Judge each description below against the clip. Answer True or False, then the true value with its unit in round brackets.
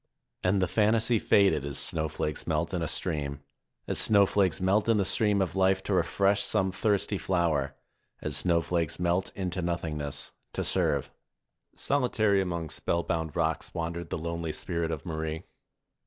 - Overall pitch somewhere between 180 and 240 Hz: False (85 Hz)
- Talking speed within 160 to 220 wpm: False (150 wpm)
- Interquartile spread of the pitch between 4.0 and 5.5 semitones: False (3.4 semitones)